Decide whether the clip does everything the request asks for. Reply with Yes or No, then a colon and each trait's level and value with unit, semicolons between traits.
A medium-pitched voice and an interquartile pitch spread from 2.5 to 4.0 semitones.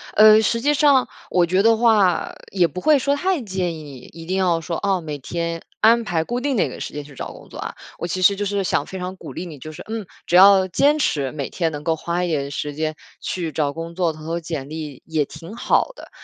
No: medium, 175 Hz; average, 4.6 semitones